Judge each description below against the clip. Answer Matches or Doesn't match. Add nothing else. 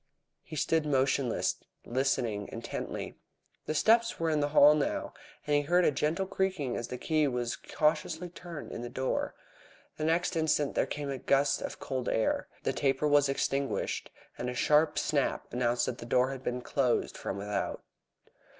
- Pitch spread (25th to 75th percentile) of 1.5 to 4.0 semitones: Matches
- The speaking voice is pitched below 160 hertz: Matches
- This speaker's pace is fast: Doesn't match